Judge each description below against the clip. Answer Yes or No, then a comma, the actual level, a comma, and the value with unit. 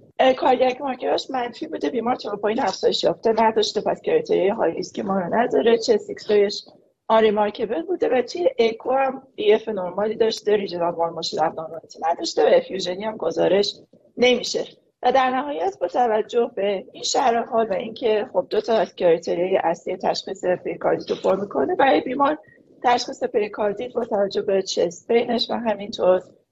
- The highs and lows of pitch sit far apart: No, average, 4.6 semitones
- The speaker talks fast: Yes, fast, 170 wpm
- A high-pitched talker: Yes, high, 225 Hz